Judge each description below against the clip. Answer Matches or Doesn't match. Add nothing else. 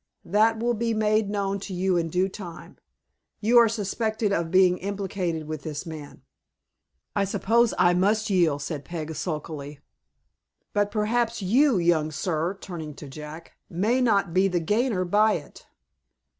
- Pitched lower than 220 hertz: Matches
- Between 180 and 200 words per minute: Doesn't match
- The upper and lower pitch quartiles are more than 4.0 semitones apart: Matches